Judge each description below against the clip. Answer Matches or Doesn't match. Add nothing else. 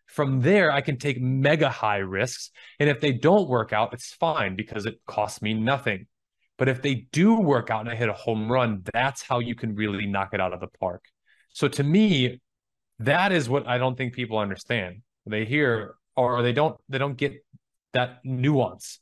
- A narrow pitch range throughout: Doesn't match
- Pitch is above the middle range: Doesn't match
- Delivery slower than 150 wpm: Doesn't match